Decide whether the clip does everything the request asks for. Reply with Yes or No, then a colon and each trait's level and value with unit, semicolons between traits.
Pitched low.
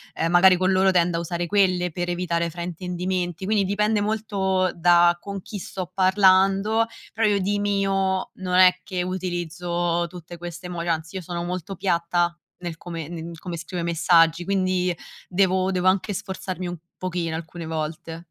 No: medium, 180 Hz